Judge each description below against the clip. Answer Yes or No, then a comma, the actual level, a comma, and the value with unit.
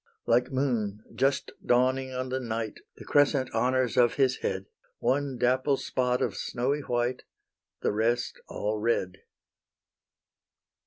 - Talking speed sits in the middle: No, slow, 125 wpm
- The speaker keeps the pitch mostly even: Yes, narrow, 2.1 semitones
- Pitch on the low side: Yes, low, 125 Hz